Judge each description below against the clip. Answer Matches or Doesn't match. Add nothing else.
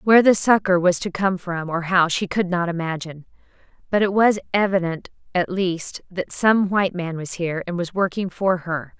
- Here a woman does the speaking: Matches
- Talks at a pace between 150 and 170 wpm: Doesn't match